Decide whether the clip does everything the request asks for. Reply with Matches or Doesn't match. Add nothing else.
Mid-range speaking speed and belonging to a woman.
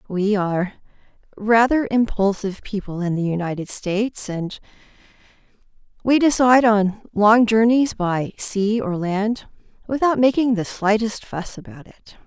Doesn't match